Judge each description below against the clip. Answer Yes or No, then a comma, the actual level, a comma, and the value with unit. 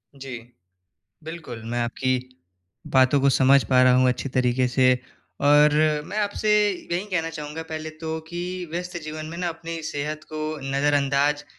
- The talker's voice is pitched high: No, medium, 150 Hz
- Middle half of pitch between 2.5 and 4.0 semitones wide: Yes, average, 3.7 semitones